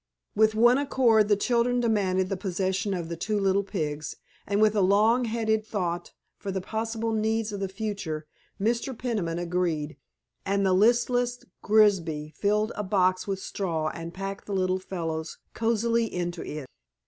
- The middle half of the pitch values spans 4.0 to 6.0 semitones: No, average, 3.4 semitones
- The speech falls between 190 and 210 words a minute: No, average, 160 wpm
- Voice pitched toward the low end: No, high, 200 Hz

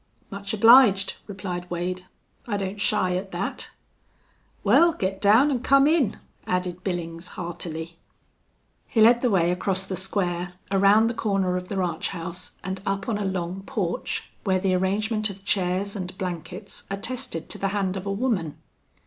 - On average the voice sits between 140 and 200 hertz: Yes, high, 190 Hz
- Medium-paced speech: Yes, average, 165 wpm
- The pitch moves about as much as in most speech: No, narrow, 2.3 semitones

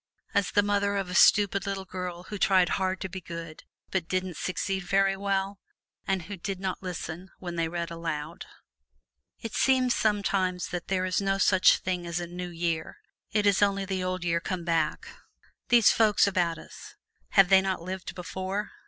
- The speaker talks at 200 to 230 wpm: No, average, 185 wpm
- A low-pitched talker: No, medium, 185 Hz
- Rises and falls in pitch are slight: Yes, narrow, 2.1 semitones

